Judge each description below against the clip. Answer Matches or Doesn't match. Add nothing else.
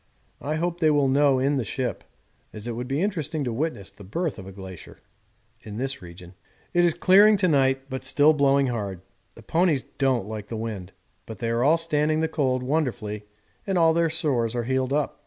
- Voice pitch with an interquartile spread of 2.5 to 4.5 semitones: Doesn't match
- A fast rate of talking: Matches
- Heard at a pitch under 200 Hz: Matches